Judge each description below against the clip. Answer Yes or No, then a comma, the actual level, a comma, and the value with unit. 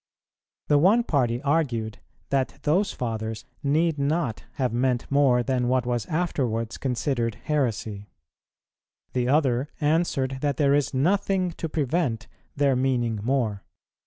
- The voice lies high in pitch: No, low, 135 Hz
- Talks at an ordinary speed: No, slow, 130 wpm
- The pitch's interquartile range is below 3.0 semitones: No, average, 3.8 semitones